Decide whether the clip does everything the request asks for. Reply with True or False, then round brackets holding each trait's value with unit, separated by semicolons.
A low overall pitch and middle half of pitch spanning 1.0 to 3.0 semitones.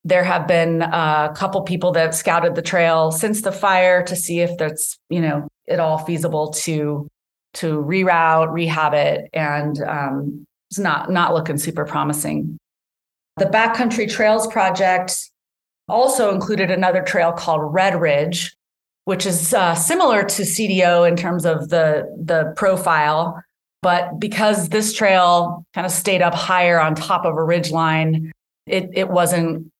False (170 Hz; 2.7 semitones)